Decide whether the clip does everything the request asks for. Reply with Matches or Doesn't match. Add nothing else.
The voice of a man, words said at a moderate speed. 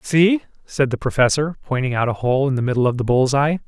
Doesn't match